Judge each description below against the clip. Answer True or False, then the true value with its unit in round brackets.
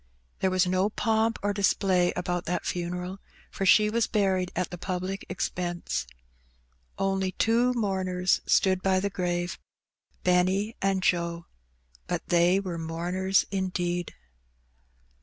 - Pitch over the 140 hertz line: True (185 Hz)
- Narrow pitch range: True (1.6 semitones)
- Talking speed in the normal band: False (125 wpm)